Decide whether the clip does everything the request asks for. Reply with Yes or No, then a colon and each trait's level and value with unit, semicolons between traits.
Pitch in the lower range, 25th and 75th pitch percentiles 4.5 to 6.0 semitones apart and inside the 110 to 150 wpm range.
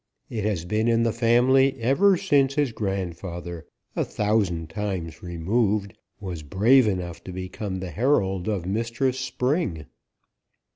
Yes: low, 105 Hz; average, 5.2 semitones; slow, 135 wpm